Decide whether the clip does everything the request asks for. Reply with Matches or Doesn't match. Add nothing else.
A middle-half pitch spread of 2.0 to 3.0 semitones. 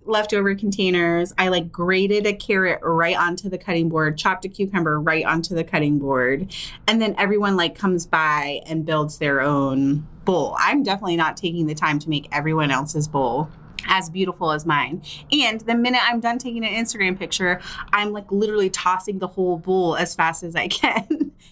Doesn't match